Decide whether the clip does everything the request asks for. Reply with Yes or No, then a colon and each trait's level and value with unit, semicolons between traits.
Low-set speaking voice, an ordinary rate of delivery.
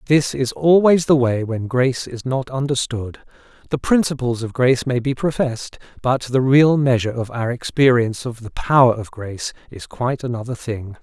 Yes: low, 125 Hz; average, 180 wpm